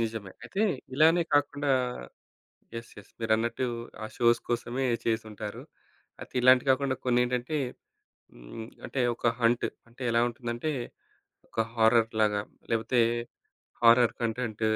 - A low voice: Yes, low, 120 Hz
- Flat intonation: Yes, narrow, 2.1 semitones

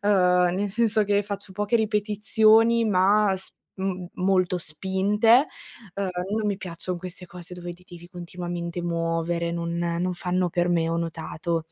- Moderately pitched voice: Yes, medium, 180 Hz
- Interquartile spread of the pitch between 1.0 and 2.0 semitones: No, narrow, 2.5 semitones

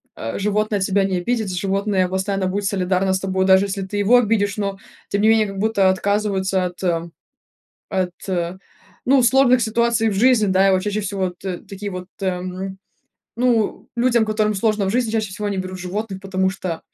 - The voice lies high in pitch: Yes, high, 200 Hz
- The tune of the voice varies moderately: No, narrow, 2.3 semitones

